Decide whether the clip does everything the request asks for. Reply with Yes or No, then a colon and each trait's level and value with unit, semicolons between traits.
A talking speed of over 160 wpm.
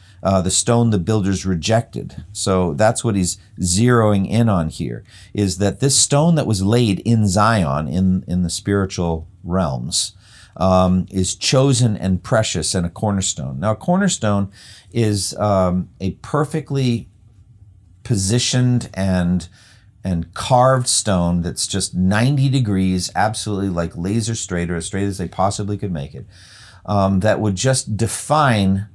No: average, 145 wpm